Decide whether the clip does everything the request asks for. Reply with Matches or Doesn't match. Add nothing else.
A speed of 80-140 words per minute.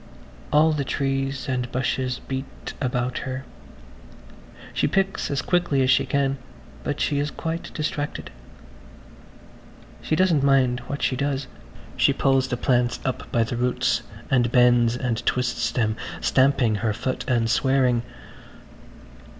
Matches